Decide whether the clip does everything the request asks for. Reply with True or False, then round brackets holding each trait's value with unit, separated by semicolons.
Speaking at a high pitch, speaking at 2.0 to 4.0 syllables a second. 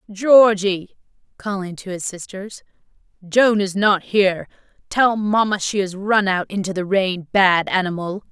True (195 Hz; 3.8 syllables/s)